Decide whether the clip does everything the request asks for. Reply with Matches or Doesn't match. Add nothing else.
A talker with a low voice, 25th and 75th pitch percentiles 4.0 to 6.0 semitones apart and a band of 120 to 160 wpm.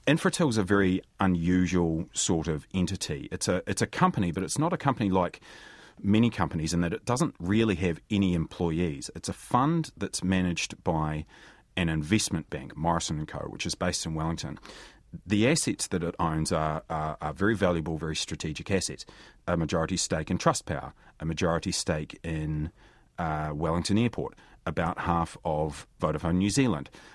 Doesn't match